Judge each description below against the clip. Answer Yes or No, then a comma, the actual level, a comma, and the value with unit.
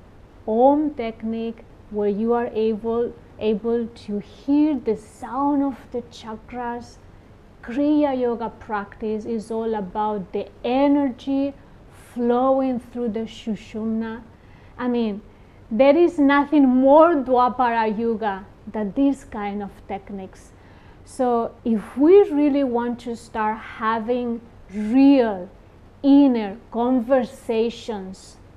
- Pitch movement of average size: Yes, average, 3.3 semitones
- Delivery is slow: Yes, slow, 105 wpm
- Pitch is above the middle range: Yes, high, 230 Hz